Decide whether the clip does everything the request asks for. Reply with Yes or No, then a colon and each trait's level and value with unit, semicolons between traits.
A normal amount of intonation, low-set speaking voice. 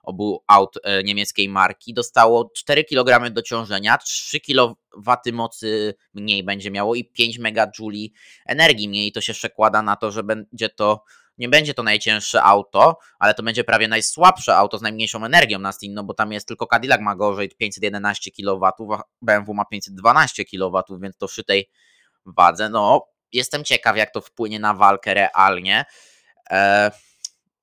No: narrow, 2.1 semitones; low, 105 Hz